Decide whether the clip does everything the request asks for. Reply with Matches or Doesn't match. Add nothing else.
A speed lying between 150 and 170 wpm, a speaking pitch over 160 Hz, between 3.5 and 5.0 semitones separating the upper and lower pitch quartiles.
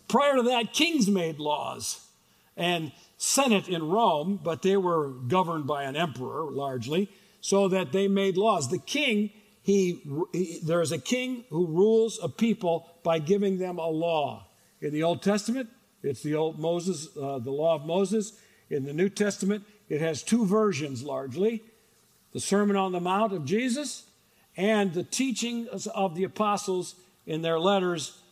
Matches